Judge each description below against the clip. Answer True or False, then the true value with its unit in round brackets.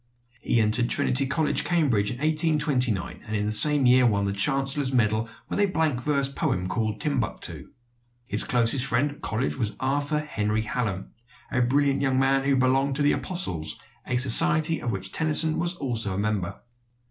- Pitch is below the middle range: True (130 Hz)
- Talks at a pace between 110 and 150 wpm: False (175 wpm)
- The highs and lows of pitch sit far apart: False (5.0 semitones)